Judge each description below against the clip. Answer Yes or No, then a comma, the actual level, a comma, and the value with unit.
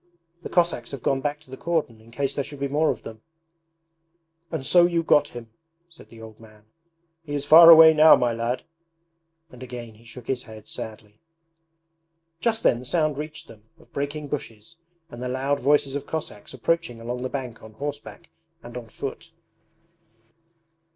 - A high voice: No, low, 135 Hz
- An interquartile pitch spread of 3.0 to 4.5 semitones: No, average, 4.9 semitones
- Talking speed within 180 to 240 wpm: Yes, average, 185 wpm